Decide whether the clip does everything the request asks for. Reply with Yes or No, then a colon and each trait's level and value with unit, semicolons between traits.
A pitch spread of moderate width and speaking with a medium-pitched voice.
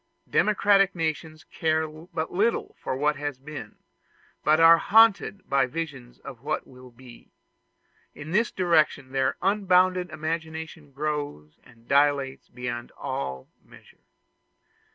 Yes: average, 4.0 semitones; medium, 155 Hz